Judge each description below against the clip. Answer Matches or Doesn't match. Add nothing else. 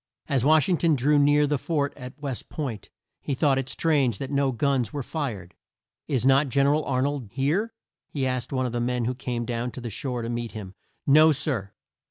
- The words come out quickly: Matches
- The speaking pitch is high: Doesn't match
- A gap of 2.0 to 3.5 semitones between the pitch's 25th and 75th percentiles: Matches